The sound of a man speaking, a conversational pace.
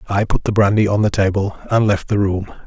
No: male; fast, 250 wpm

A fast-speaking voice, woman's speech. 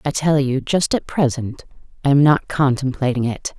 No: average, 185 wpm; female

